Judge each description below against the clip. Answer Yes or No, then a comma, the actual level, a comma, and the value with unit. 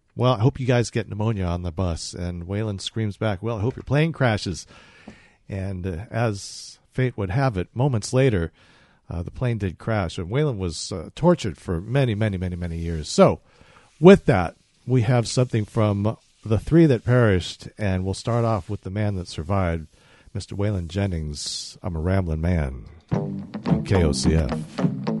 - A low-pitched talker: Yes, low, 105 Hz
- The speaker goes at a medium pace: Yes, average, 175 wpm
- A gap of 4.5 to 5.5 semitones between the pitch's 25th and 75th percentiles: Yes, average, 5.1 semitones